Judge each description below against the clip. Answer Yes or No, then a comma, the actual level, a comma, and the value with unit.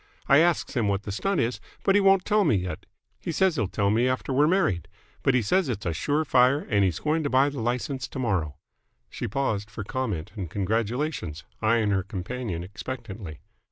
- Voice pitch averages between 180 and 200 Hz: No, low, 120 Hz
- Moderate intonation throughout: No, wide, 6.1 semitones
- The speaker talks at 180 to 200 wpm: Yes, average, 195 wpm